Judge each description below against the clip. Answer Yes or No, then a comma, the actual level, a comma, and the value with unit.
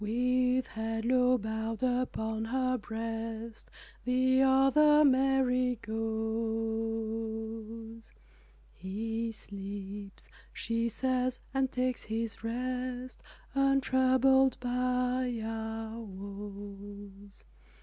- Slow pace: Yes, slow, 75 wpm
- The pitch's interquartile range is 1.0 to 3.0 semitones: Yes, narrow, 2.4 semitones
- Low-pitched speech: No, high, 230 Hz